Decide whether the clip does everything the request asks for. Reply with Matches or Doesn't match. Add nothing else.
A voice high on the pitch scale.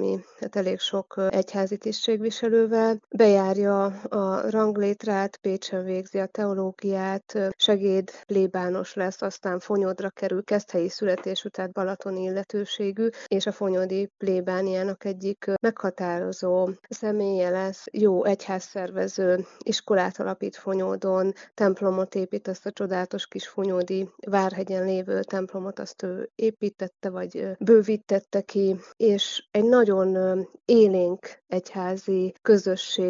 Matches